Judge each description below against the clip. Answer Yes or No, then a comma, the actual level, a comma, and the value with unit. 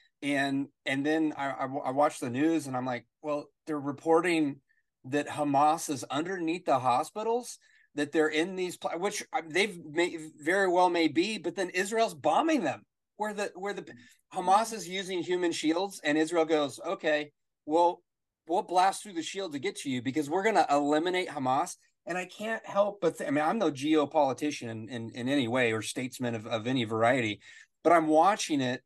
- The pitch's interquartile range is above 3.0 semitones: Yes, average, 4.3 semitones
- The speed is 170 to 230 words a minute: Yes, average, 190 wpm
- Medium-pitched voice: Yes, medium, 155 Hz